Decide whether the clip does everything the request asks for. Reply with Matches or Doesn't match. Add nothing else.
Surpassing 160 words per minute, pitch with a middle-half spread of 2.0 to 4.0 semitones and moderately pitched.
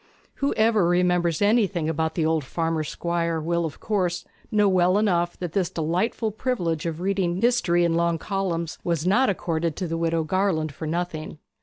Matches